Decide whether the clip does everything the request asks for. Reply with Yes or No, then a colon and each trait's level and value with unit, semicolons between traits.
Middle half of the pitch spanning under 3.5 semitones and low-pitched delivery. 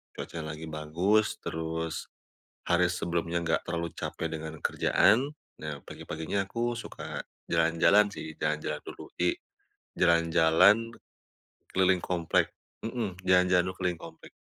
Yes: average, 2.8 semitones; very low, 85 Hz